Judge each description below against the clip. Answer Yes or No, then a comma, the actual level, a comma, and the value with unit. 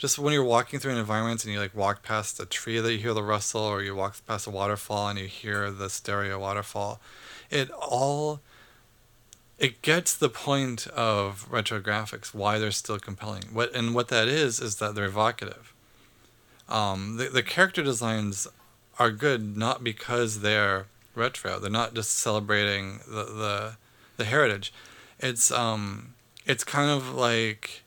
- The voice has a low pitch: Yes, low, 110 Hz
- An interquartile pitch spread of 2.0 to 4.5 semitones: Yes, average, 2.8 semitones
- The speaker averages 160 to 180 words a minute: Yes, average, 170 wpm